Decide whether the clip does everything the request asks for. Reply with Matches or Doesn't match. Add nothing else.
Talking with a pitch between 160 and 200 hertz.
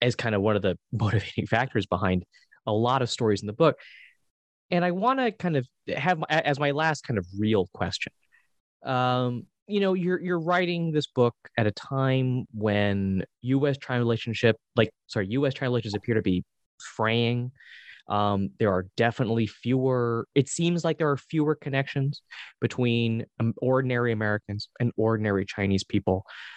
Doesn't match